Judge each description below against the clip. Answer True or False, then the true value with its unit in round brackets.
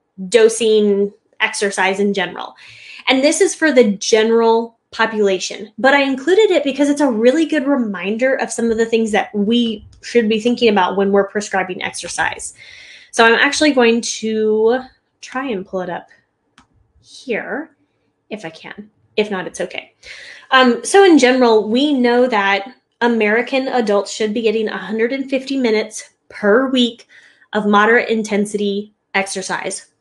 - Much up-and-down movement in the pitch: False (3.6 semitones)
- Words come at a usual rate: True (150 wpm)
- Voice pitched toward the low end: False (225 Hz)